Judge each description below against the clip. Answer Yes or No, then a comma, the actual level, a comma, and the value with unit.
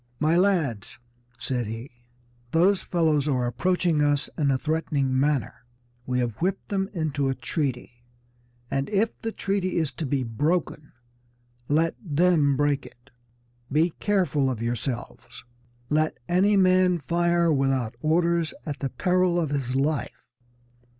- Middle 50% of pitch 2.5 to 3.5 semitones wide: No, average, 4.7 semitones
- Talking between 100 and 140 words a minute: Yes, slow, 135 wpm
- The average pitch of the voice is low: No, medium, 150 Hz